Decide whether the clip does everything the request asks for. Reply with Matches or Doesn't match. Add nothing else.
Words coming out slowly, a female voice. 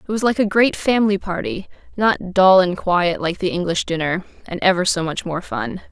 Doesn't match